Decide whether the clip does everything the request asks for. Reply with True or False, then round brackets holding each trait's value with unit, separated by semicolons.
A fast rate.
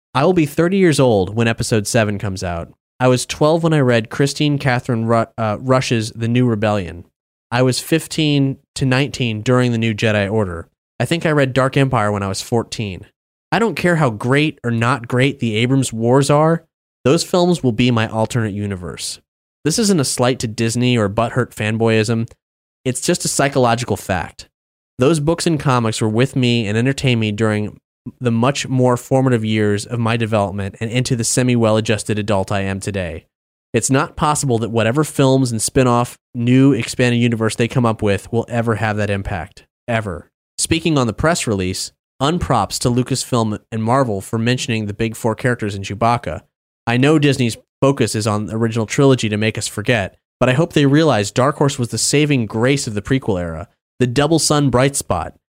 False (190 wpm)